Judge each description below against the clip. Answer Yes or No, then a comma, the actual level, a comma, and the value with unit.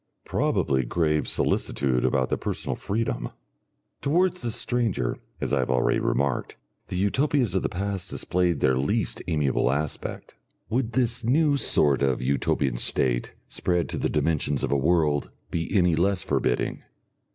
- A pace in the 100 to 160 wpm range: Yes, average, 150 wpm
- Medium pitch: No, very low, 85 Hz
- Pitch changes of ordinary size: No, wide, 8.2 semitones